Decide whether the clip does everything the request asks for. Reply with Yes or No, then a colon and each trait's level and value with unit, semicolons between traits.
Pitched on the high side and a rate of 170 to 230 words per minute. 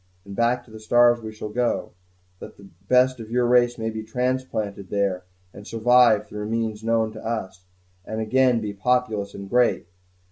No: low, 110 Hz; average, 180 wpm